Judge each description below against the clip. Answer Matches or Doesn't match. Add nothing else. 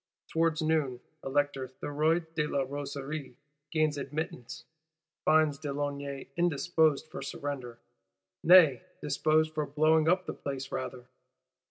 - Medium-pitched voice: Matches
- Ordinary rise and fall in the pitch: Doesn't match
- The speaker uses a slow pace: Matches